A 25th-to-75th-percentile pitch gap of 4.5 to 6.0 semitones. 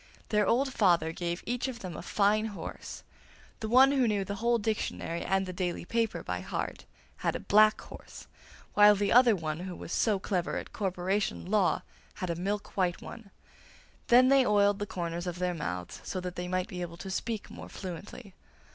No: average, 3.4 semitones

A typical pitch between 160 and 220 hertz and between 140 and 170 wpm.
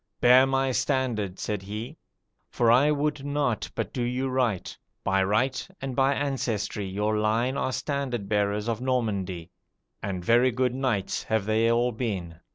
No: low, 120 Hz; average, 160 wpm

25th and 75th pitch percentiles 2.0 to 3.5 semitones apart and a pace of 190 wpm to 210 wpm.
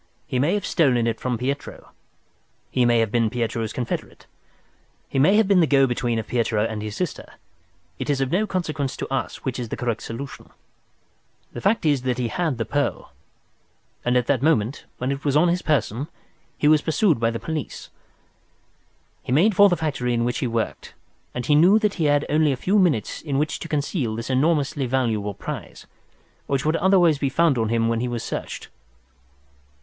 No: average, 4.9 semitones; average, 200 wpm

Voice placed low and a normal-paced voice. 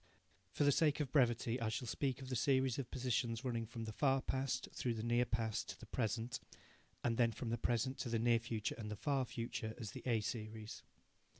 No: low, 120 Hz; fast, 220 wpm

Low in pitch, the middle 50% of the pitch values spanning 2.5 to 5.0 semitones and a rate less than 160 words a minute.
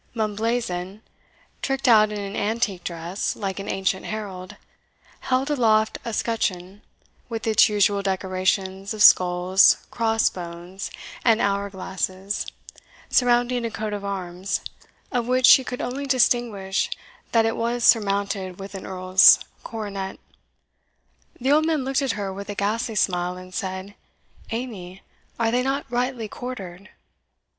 No: high, 205 Hz; average, 3.6 semitones; slow, 135 wpm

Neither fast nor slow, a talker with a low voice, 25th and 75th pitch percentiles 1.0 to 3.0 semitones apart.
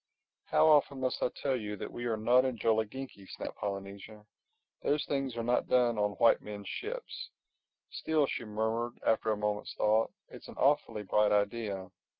No: average, 165 wpm; low, 115 Hz; average, 3.6 semitones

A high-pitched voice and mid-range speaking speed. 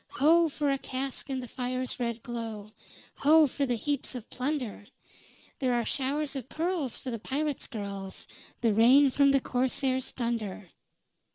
Yes: very high, 255 Hz; average, 160 wpm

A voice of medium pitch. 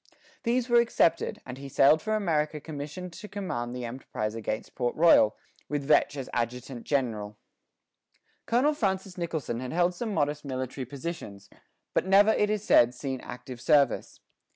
Yes: medium, 145 Hz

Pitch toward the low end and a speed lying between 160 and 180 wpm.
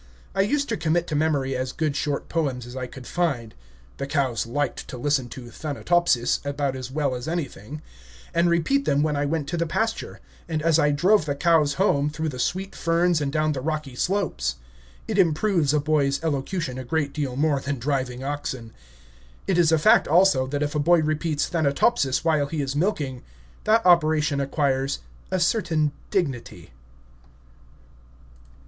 No: medium, 150 Hz; average, 175 wpm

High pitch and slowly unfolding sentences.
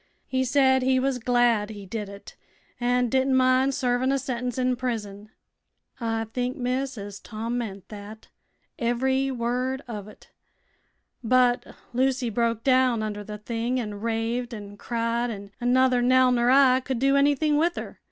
No: high, 245 Hz; average, 160 wpm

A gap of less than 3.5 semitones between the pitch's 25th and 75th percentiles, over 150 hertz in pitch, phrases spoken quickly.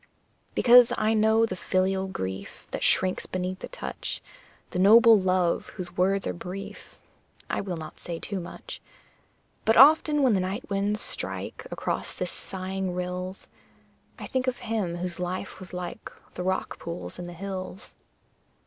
No: average, 3.0 semitones; high, 190 Hz; average, 160 wpm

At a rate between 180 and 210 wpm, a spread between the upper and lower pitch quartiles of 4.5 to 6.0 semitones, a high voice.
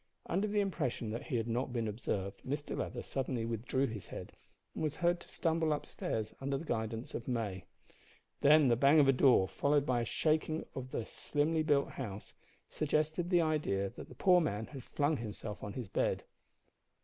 No: average, 195 wpm; wide, 5.4 semitones; low, 135 Hz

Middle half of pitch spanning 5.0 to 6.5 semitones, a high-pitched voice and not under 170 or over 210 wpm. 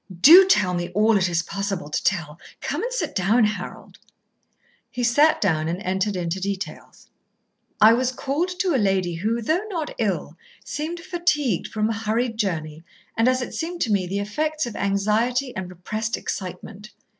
Yes: wide, 5.6 semitones; high, 215 Hz; average, 175 wpm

